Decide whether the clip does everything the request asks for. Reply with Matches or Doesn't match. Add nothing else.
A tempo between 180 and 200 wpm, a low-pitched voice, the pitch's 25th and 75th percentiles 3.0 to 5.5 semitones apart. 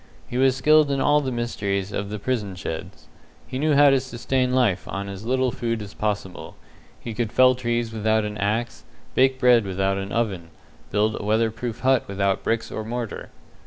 Matches